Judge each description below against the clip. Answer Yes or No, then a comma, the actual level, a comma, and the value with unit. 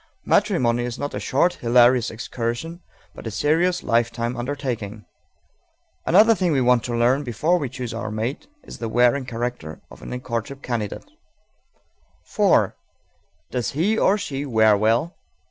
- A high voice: No, low, 125 Hz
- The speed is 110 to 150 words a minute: Yes, average, 145 wpm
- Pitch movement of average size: Yes, average, 3.6 semitones